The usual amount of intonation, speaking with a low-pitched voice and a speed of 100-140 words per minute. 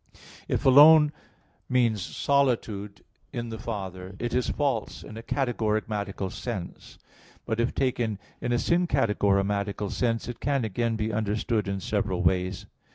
Yes: average, 3.4 semitones; low, 110 Hz; slow, 135 wpm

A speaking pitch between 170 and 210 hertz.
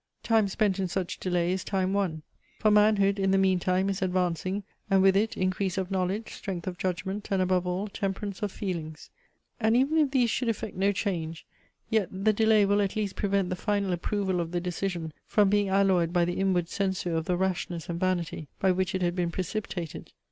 Yes: high, 190 Hz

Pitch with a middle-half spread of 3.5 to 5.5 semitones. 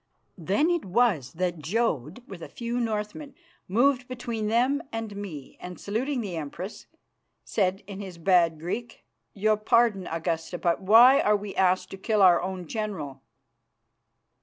Yes: average, 4.7 semitones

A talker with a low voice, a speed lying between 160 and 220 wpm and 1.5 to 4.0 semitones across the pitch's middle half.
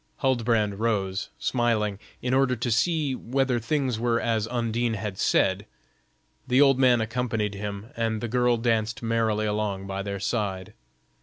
No: low, 115 Hz; average, 150 wpm; average, 2.8 semitones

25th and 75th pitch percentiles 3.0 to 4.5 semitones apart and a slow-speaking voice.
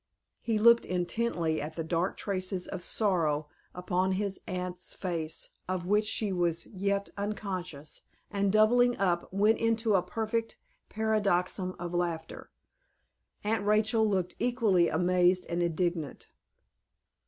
Yes: average, 3.3 semitones; slow, 125 wpm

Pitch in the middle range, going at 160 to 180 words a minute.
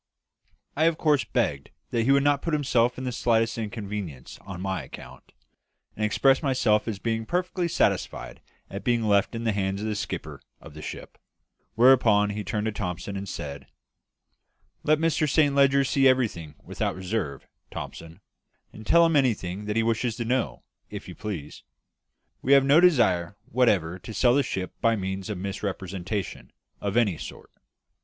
No: low, 110 Hz; average, 170 wpm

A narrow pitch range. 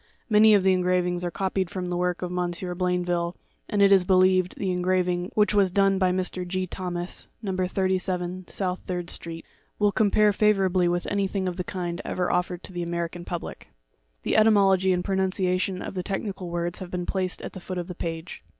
Yes: narrow, 1.4 semitones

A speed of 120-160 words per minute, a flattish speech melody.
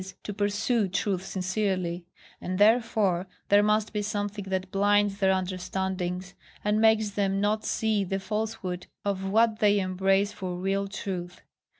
Yes: average, 140 wpm; narrow, 1.9 semitones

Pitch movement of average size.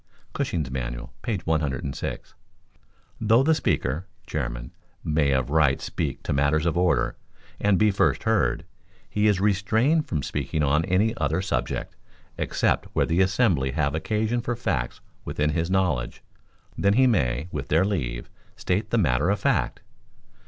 No: wide, 6.7 semitones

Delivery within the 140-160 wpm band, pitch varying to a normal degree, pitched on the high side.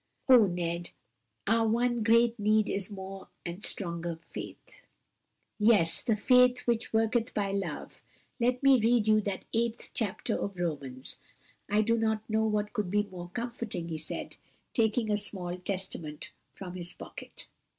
Yes: average, 150 wpm; average, 4.1 semitones; high, 210 Hz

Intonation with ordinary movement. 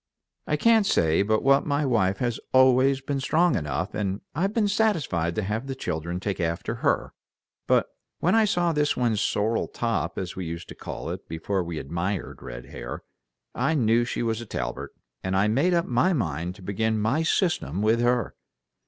No: wide, 7.3 semitones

